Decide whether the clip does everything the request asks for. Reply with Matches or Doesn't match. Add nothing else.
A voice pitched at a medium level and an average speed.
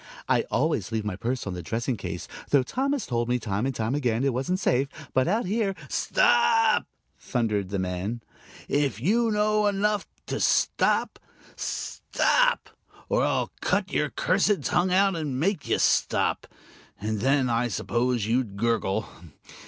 Doesn't match